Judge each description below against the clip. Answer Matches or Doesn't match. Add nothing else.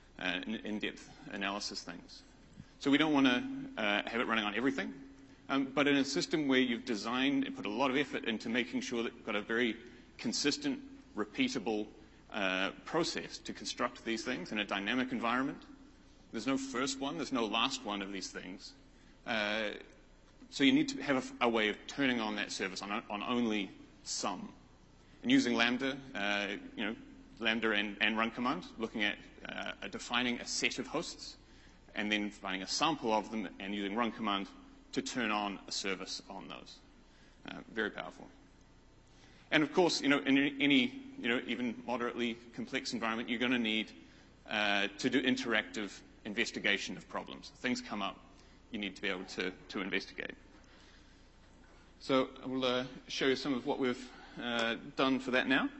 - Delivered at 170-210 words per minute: Matches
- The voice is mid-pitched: Doesn't match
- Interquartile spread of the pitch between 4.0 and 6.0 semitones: Matches